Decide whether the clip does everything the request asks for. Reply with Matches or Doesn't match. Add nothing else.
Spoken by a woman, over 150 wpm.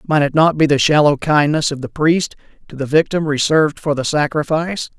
Doesn't match